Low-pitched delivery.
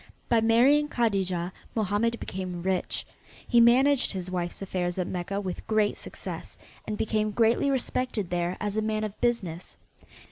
No: high, 210 Hz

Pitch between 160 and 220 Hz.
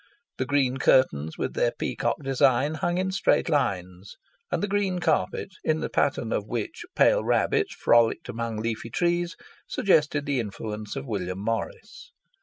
No: low, 135 Hz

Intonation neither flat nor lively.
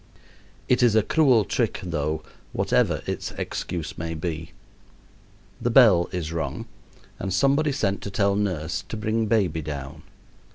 No: wide, 5.8 semitones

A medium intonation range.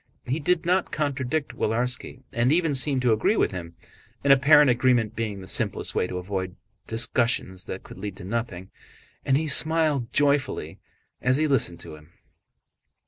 No: wide, 6.5 semitones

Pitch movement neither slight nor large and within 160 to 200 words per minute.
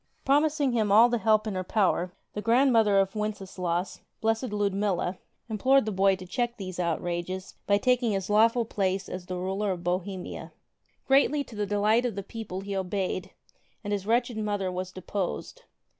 Yes: average, 3.3 semitones; average, 175 wpm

